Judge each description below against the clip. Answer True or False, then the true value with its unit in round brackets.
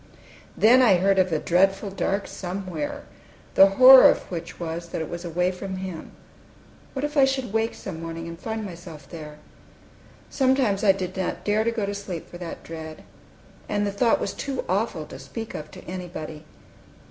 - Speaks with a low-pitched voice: False (190 Hz)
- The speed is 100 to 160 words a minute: False (185 wpm)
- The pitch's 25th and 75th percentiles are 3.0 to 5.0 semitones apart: True (4.1 semitones)